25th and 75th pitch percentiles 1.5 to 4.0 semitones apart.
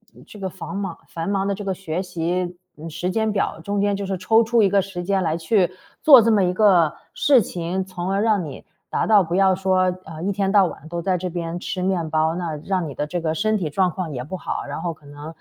Yes: average, 3.0 semitones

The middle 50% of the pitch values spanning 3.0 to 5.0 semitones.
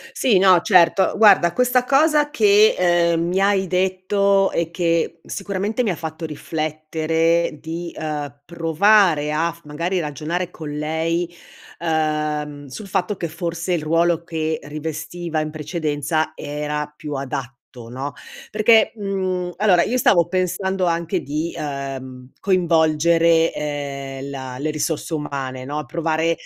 Yes: average, 3.4 semitones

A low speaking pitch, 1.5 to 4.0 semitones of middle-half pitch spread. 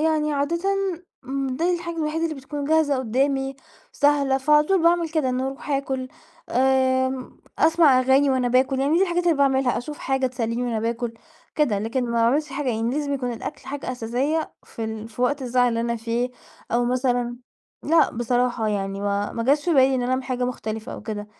No: very high, 260 Hz; average, 3.3 semitones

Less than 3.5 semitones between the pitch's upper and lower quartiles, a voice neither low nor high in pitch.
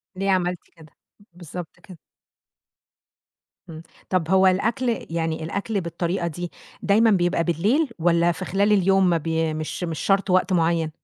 Yes: average, 2.9 semitones; medium, 175 Hz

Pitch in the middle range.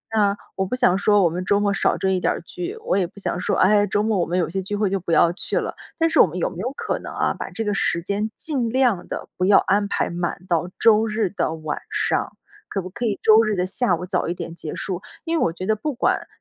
No: high, 200 Hz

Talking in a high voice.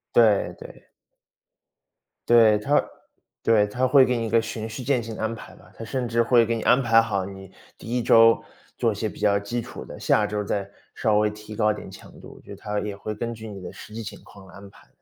No: low, 110 Hz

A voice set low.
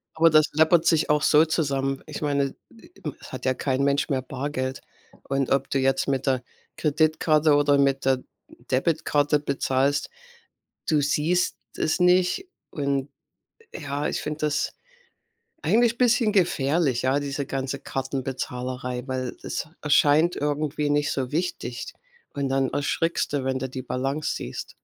No: medium, 145 Hz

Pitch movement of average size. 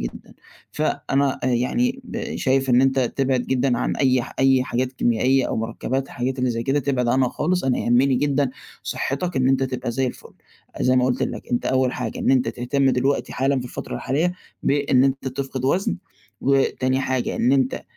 No: narrow, 1.4 semitones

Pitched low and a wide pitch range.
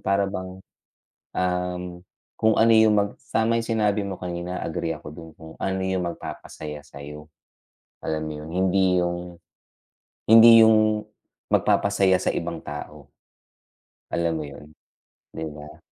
No: very low, 90 Hz; average, 3.8 semitones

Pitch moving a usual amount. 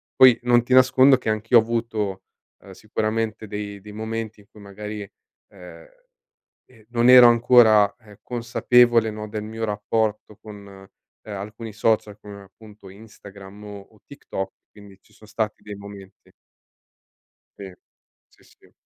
No: narrow, 2.0 semitones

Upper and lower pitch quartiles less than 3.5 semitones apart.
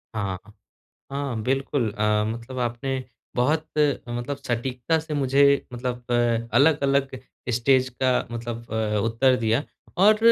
Yes: average, 2.8 semitones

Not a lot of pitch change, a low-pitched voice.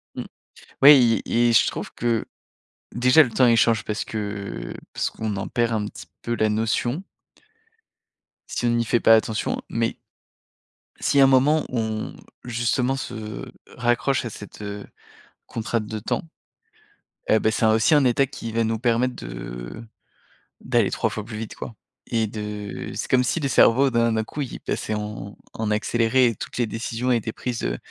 Yes: narrow, 2.3 semitones; low, 115 Hz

